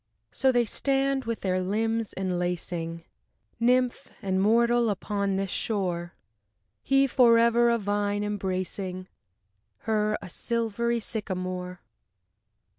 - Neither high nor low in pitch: No, high, 210 Hz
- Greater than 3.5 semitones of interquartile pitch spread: Yes, average, 4.0 semitones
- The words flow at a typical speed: No, slow, 105 wpm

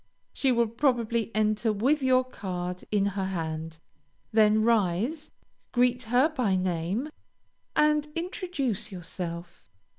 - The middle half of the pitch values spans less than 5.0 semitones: No, wide, 5.4 semitones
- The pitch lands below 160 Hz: No, high, 220 Hz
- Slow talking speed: Yes, slow, 115 wpm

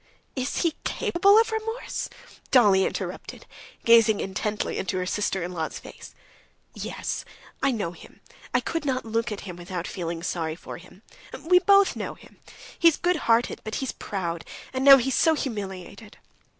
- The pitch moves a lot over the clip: Yes, wide, 7.3 semitones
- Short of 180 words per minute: Yes, average, 165 wpm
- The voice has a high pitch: Yes, high, 225 Hz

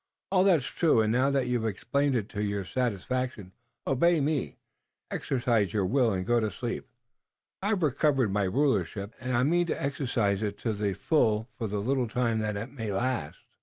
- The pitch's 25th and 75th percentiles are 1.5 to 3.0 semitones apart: No, average, 4.7 semitones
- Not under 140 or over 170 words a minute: No, average, 190 wpm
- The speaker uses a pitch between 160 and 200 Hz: No, low, 120 Hz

